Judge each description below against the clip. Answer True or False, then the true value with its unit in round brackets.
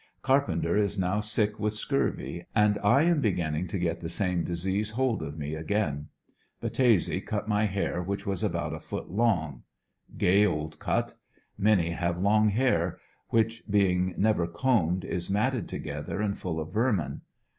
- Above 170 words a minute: False (160 wpm)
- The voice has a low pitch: True (100 Hz)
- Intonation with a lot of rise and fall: False (4.0 semitones)